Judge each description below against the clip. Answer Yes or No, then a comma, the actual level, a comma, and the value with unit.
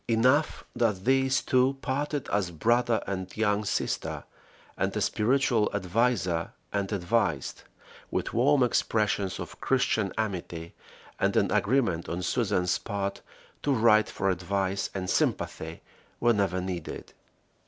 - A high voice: No, low, 105 Hz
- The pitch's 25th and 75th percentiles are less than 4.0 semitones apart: No, average, 4.9 semitones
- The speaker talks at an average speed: No, slow, 120 wpm